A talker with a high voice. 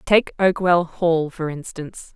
No: medium, 170 Hz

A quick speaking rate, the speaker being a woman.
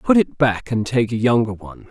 No: fast, 250 wpm; male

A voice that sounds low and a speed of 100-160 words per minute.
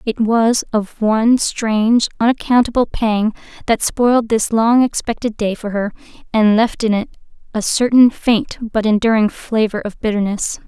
No: high, 225 Hz; average, 150 wpm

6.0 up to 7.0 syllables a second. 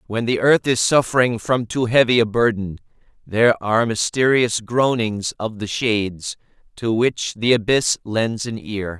No: 4.5 syllables/s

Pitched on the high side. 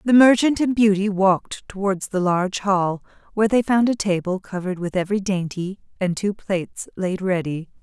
Yes: high, 195 Hz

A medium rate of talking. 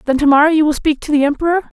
No: fast, 270 wpm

